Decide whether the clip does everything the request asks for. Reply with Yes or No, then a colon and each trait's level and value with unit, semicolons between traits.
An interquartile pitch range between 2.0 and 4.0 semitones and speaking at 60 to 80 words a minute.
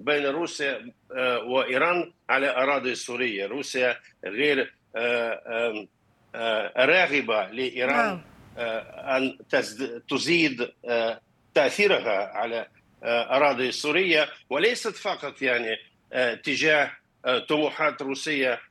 Yes: average, 2.9 semitones; average, 70 wpm